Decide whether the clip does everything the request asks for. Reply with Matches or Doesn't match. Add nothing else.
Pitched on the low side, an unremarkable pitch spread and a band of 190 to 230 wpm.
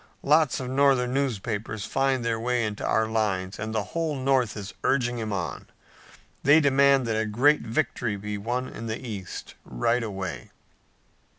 Doesn't match